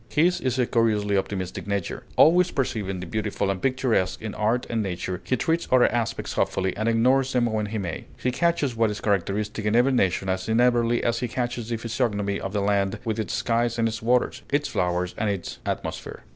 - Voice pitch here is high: No, low, 110 Hz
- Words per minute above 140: Yes, fast, 205 wpm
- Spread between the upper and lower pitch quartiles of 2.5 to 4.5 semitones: Yes, average, 3.5 semitones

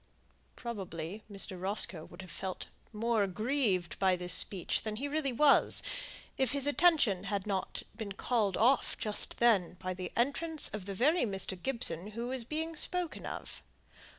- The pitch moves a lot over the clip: Yes, wide, 5.9 semitones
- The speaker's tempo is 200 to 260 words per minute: No, average, 160 wpm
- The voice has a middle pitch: No, high, 215 Hz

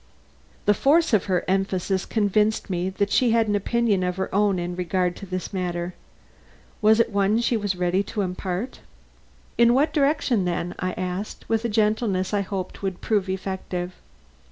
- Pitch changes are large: No, average, 3.0 semitones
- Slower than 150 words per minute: No, average, 175 wpm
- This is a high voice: Yes, high, 195 Hz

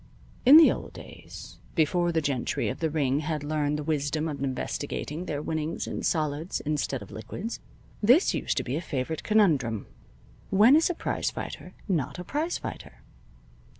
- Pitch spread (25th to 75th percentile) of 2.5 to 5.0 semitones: Yes, average, 3.8 semitones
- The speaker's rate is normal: Yes, average, 170 wpm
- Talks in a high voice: No, medium, 155 Hz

